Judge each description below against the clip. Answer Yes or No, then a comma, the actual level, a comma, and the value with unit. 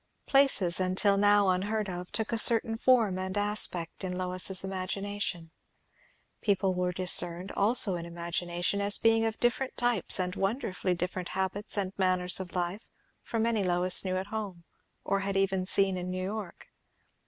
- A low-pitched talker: No, high, 190 Hz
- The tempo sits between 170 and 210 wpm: No, average, 160 wpm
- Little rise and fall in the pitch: Yes, narrow, 2.2 semitones